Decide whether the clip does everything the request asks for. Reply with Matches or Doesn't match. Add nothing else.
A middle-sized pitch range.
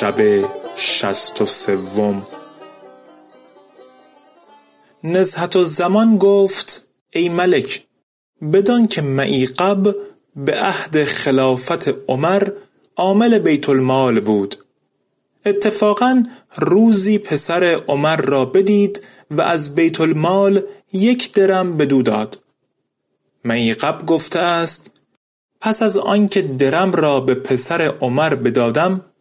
Doesn't match